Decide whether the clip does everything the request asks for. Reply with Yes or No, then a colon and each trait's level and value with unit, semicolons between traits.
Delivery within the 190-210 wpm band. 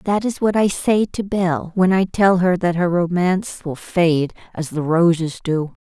Yes: fast, 205 wpm